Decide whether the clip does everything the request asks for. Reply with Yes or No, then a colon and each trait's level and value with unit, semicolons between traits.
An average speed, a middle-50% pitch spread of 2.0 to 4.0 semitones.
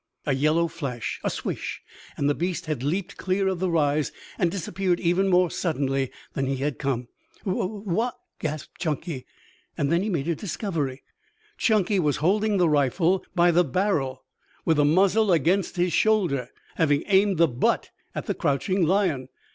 No: average, 170 wpm; average, 4.7 semitones